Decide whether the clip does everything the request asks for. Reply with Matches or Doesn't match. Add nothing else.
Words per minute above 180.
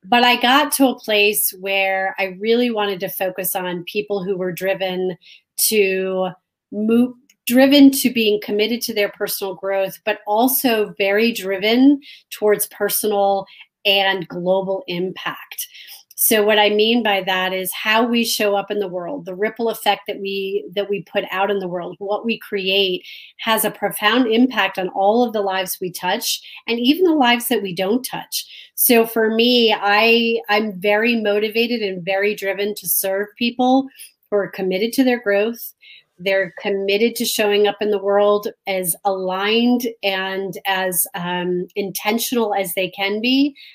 Doesn't match